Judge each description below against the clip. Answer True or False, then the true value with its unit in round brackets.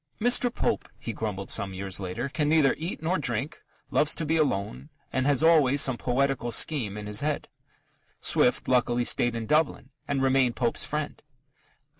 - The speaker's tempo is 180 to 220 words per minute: False (170 wpm)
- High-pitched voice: False (135 Hz)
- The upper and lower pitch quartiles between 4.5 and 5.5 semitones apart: True (4.8 semitones)